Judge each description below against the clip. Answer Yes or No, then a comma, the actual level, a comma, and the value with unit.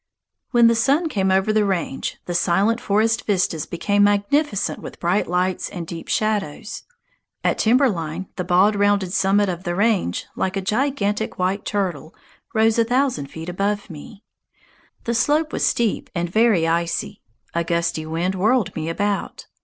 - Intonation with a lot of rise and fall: No, average, 4.0 semitones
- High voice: Yes, high, 200 Hz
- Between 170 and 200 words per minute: No, average, 160 wpm